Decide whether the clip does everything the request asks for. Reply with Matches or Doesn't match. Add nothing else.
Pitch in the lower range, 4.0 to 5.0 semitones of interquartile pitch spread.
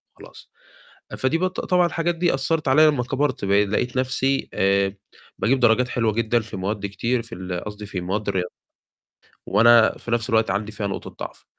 Matches